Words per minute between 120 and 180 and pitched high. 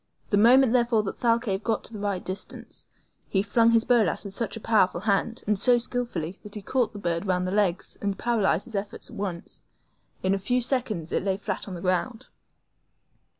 No: fast, 205 wpm; high, 205 Hz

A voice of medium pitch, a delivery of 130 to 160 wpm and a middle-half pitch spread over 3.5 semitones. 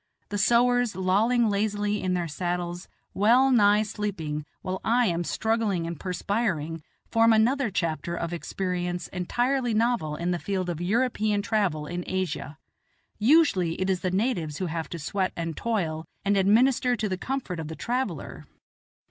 No: high, 195 Hz; average, 155 wpm; average, 4.6 semitones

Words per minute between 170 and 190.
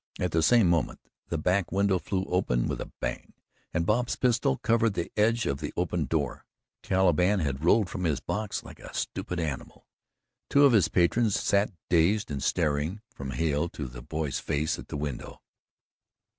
Yes: average, 180 wpm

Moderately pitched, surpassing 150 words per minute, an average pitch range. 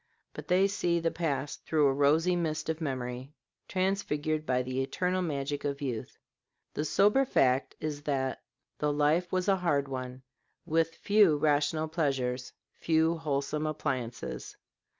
No: medium, 150 Hz; average, 145 wpm; average, 3.3 semitones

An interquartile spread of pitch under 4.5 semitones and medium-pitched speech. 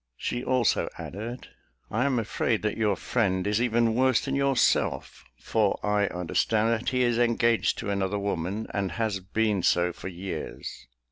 No: average, 3.2 semitones; low, 110 Hz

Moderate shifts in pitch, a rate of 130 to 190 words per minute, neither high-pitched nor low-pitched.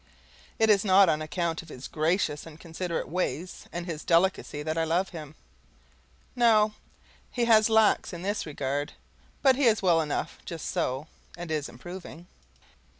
Yes: average, 4.2 semitones; average, 160 wpm; medium, 170 Hz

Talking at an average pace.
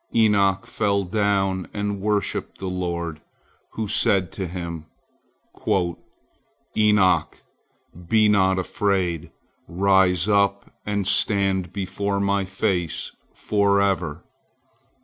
No: slow, 90 wpm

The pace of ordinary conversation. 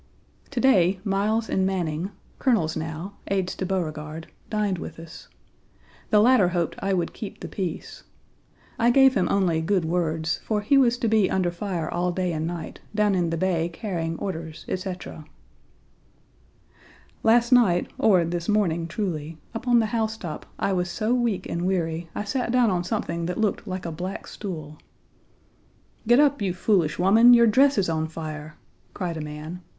Yes: average, 170 wpm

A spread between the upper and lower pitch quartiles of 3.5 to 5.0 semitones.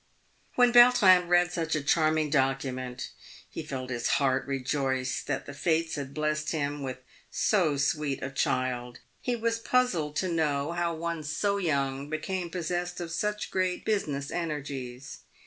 Yes: average, 4.3 semitones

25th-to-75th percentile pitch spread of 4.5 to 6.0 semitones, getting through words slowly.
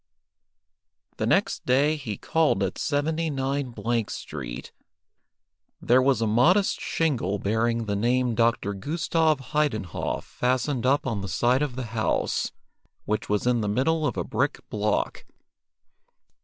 Yes: average, 5.1 semitones; slow, 130 wpm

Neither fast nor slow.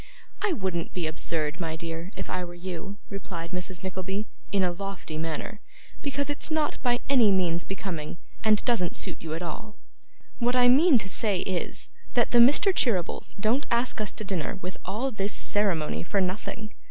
Yes: average, 180 wpm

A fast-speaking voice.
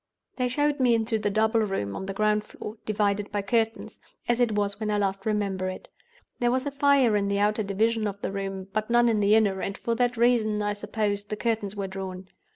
Yes: fast, 225 wpm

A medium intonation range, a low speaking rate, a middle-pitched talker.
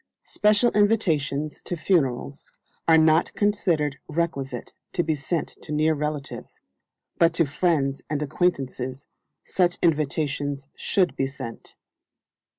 Yes: average, 3.8 semitones; slow, 115 wpm; medium, 155 Hz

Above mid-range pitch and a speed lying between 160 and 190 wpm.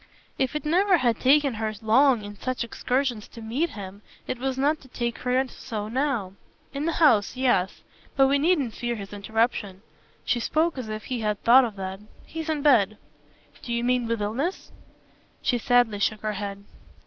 Yes: high, 240 Hz; average, 185 wpm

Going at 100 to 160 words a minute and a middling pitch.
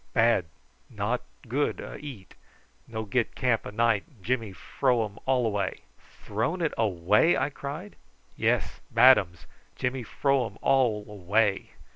No: average, 140 wpm; low, 115 Hz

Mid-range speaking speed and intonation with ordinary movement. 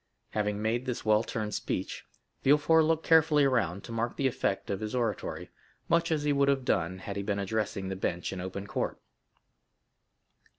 No: average, 180 wpm; wide, 5.8 semitones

